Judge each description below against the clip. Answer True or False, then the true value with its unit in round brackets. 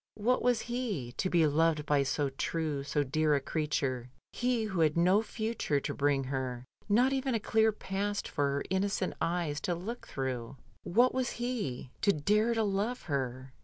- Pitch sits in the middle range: True (170 Hz)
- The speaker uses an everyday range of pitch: False (7.6 semitones)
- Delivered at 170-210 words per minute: True (185 wpm)